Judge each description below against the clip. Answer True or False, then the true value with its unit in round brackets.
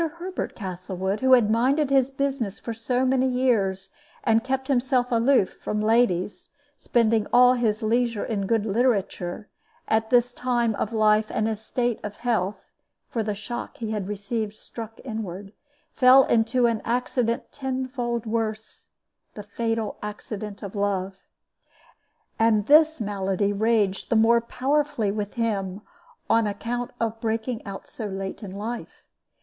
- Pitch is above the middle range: True (225 Hz)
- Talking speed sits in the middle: True (145 wpm)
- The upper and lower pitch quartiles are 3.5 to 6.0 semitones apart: False (3.0 semitones)